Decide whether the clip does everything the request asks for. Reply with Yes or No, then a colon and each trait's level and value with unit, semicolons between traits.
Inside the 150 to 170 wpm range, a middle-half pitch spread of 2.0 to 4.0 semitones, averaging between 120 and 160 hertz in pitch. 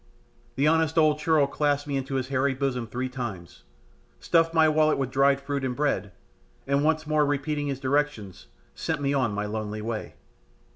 No: average, 180 wpm; average, 2.8 semitones; medium, 140 Hz